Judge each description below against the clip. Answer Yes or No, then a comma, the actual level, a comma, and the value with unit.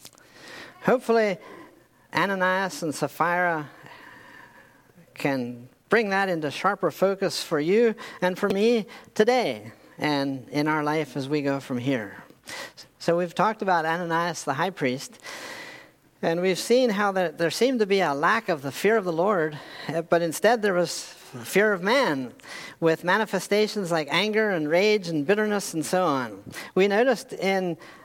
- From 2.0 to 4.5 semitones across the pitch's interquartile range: No, average, 5.0 semitones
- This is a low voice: No, medium, 180 Hz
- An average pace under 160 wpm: Yes, average, 150 wpm